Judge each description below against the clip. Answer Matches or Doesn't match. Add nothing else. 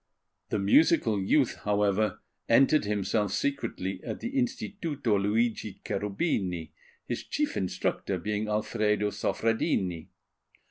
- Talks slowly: Matches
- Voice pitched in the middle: Doesn't match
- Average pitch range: Matches